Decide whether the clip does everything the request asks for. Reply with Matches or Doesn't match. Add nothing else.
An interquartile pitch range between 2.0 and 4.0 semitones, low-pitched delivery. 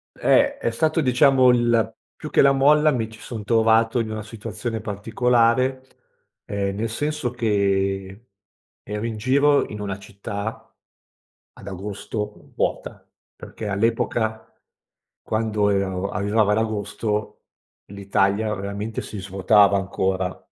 Matches